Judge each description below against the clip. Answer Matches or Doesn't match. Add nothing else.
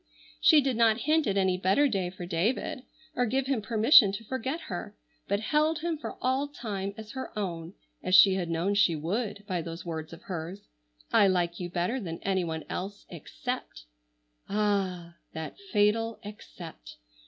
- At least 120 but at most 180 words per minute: Matches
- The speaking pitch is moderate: Doesn't match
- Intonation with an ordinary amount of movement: Matches